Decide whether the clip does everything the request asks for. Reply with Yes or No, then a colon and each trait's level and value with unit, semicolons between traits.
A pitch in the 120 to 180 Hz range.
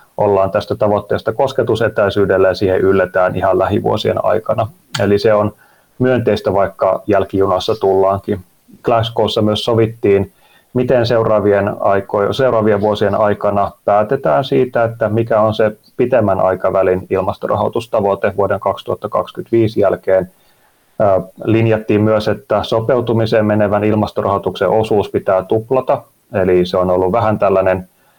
No: low, 105 Hz